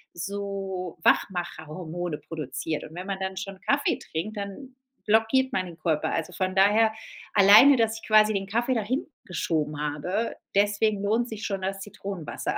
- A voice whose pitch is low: No, high, 195 Hz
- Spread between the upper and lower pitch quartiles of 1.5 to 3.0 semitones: No, average, 3.7 semitones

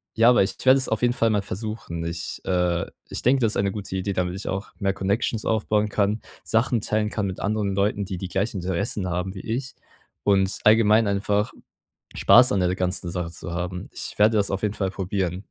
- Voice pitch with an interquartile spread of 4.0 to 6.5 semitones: No, narrow, 2.6 semitones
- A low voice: Yes, low, 100 Hz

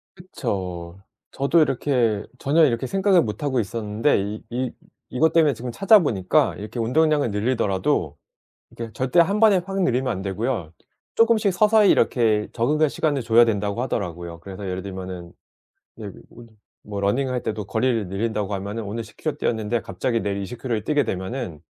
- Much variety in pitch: Yes, wide, 5.8 semitones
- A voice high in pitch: No, low, 115 Hz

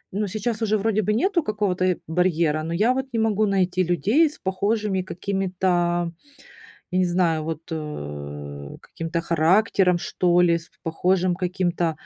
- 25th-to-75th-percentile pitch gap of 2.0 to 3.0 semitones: No, average, 3.5 semitones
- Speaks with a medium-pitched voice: Yes, medium, 180 Hz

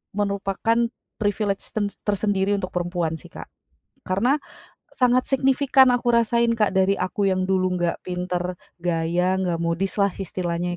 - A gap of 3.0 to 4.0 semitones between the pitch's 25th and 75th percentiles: Yes, average, 3.4 semitones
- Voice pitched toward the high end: Yes, high, 195 Hz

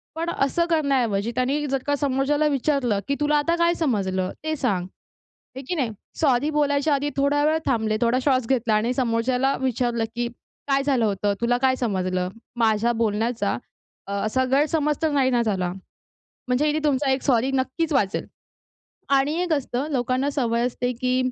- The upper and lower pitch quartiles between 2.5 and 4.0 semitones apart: Yes, average, 3.7 semitones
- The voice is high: Yes, very high, 260 Hz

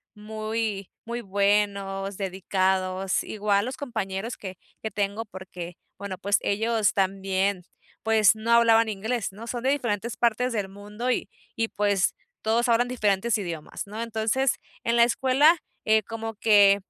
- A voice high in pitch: Yes, high, 210 Hz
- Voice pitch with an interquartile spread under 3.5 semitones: Yes, average, 2.8 semitones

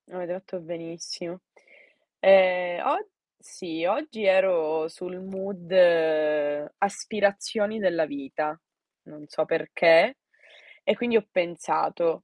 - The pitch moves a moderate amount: Yes, average, 3.0 semitones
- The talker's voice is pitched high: No, medium, 175 Hz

